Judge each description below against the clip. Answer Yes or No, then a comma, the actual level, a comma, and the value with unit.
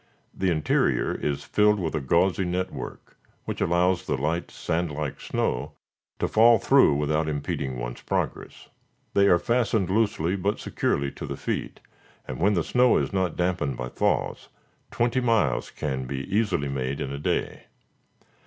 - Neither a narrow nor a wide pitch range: No, wide, 5.9 semitones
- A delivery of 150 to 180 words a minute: Yes, average, 160 wpm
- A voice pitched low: Yes, very low, 85 Hz